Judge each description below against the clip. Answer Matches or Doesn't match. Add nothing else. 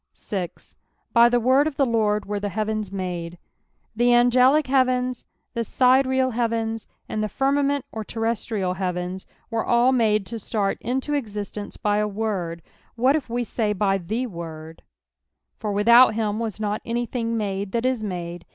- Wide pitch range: Doesn't match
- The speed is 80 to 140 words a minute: Doesn't match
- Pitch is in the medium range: Doesn't match